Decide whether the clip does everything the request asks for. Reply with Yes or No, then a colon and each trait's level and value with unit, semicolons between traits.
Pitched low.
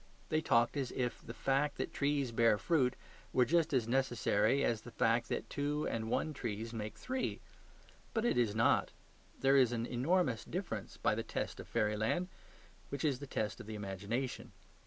Yes: low, 125 Hz